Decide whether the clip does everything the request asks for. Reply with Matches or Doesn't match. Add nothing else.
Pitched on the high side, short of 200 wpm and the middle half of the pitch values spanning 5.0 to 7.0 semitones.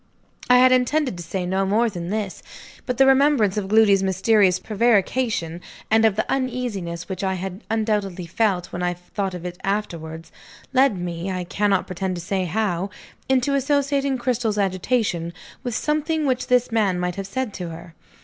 Matches